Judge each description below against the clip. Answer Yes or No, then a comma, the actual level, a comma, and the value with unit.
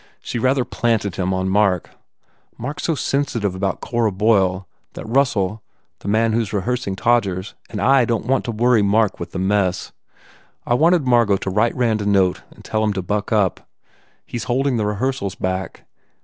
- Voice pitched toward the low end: Yes, low, 110 Hz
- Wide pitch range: No, average, 3.8 semitones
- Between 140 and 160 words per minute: No, average, 195 wpm